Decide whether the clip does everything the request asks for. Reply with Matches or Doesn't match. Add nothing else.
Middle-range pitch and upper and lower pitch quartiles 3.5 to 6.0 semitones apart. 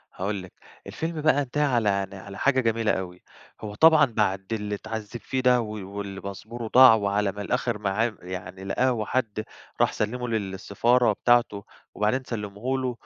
Doesn't match